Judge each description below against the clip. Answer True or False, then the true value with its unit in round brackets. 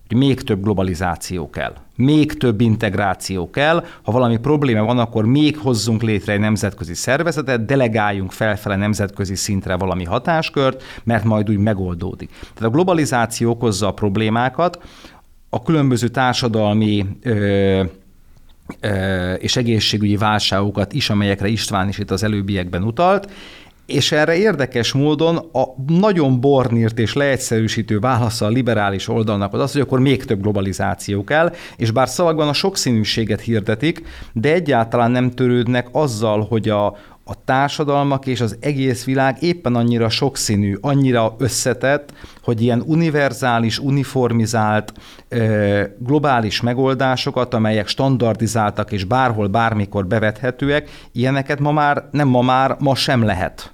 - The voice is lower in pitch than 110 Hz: False (115 Hz)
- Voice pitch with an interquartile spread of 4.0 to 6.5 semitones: True (4.4 semitones)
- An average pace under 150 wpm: True (135 wpm)